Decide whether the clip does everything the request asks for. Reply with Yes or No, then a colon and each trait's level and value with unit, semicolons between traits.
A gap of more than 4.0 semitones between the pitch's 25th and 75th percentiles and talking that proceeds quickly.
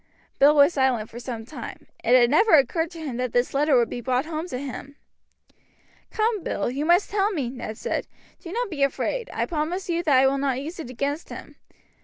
Yes: average, 5.0 semitones; fast, 220 wpm